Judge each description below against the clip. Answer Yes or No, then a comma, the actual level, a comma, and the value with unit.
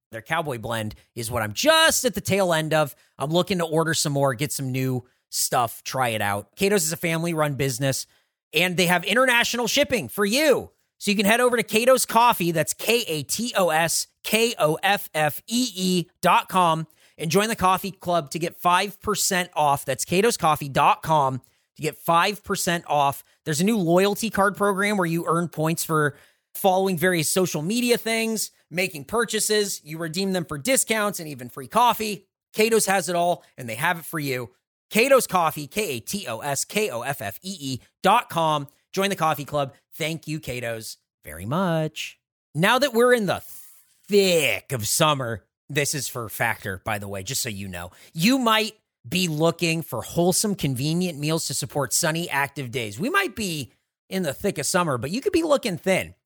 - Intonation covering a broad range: Yes, wide, 6.1 semitones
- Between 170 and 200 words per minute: Yes, average, 180 wpm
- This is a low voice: No, medium, 170 Hz